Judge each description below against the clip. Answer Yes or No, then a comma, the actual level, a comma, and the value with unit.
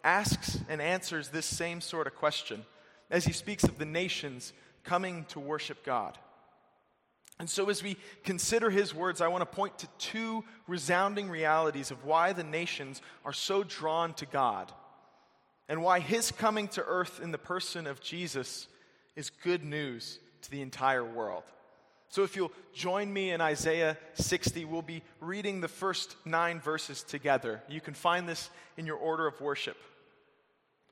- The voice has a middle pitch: Yes, medium, 165 Hz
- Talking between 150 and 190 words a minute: Yes, average, 165 wpm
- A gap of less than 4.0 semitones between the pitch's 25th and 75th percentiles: Yes, average, 3.4 semitones